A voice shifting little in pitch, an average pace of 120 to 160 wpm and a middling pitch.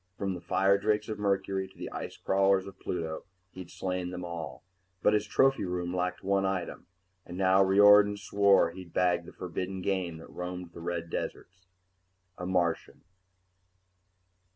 No: narrow, 1.7 semitones; average, 155 wpm; very low, 95 Hz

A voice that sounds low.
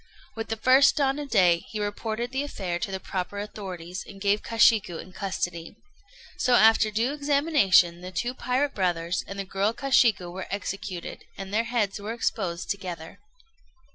No: high, 205 Hz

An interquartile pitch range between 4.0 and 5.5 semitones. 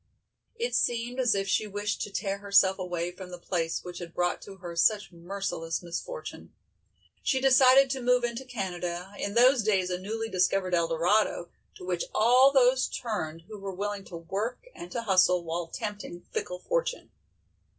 Yes: average, 5.1 semitones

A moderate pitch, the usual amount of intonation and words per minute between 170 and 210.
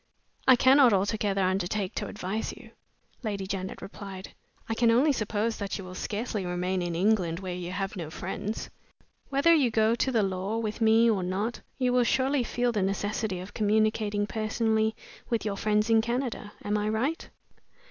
No: high, 215 Hz; average, 3.0 semitones; average, 175 wpm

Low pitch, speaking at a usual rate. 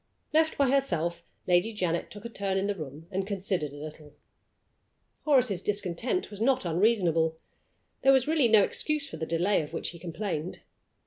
No: high, 195 Hz; average, 175 wpm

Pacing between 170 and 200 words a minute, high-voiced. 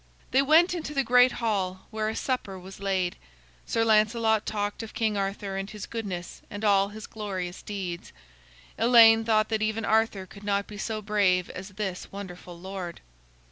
Yes: average, 175 wpm; high, 210 Hz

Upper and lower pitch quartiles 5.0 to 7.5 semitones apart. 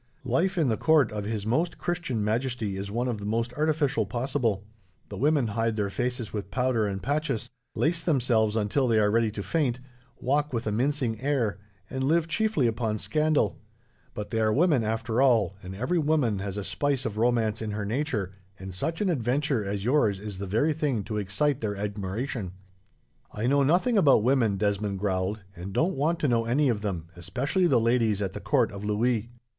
Yes: wide, 5.4 semitones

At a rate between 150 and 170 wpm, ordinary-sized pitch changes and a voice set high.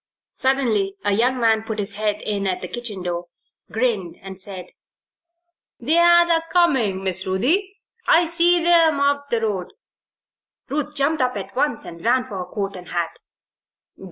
No: average, 160 wpm; wide, 6.7 semitones; high, 225 Hz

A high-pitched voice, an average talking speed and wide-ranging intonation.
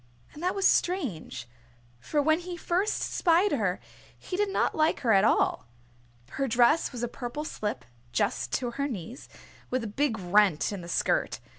Yes: very high, 255 Hz; average, 175 wpm; wide, 7.7 semitones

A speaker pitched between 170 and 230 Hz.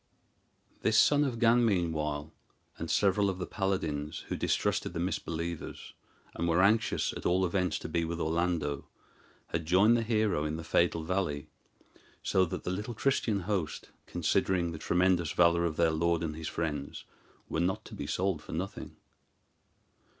No: very low, 85 Hz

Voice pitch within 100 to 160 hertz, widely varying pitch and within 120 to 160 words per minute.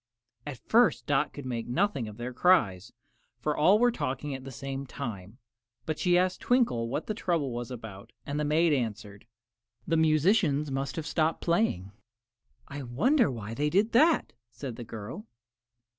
No: medium, 140 Hz; wide, 6.3 semitones; average, 170 wpm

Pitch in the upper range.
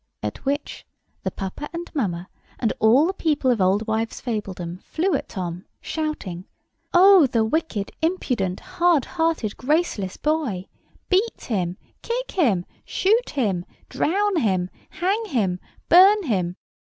Yes: very high, 260 Hz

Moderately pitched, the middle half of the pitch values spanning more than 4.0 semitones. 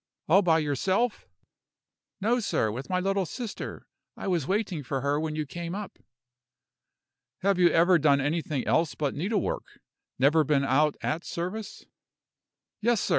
Yes: medium, 170 Hz; average, 4.9 semitones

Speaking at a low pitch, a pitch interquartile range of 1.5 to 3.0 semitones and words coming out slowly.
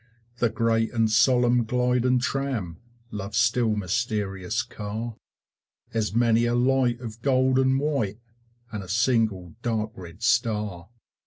Yes: low, 115 Hz; average, 2.7 semitones; slow, 130 wpm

